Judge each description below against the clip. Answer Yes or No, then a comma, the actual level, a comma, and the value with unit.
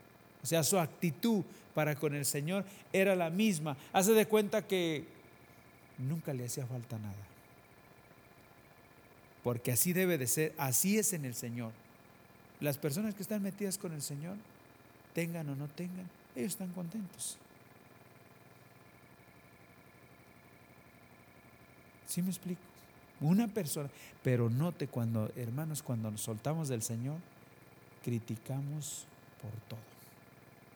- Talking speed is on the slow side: Yes, slow, 120 wpm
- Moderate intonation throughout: No, wide, 7.0 semitones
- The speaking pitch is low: No, medium, 145 Hz